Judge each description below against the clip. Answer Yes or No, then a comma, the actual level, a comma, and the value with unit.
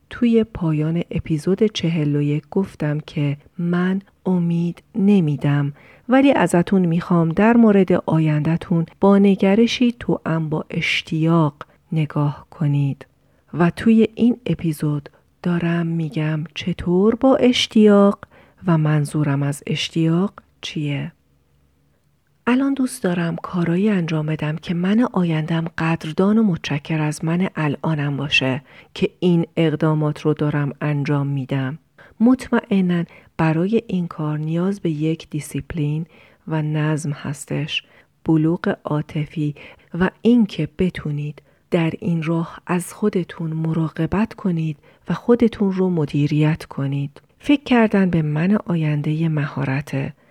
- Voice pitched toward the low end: No, medium, 165 Hz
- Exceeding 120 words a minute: No, average, 110 wpm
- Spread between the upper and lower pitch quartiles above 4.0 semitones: No, average, 3.7 semitones